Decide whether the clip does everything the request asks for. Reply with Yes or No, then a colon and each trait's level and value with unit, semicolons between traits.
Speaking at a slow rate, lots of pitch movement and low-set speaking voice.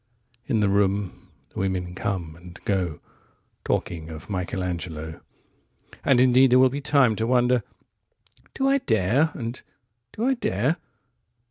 Yes: slow, 120 wpm; wide, 6.1 semitones; low, 105 Hz